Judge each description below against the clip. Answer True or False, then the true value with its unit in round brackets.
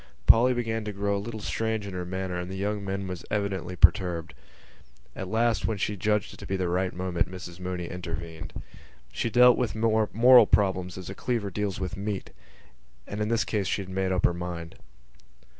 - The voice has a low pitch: True (95 Hz)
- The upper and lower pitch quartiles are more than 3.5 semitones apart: False (2.8 semitones)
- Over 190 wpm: True (200 wpm)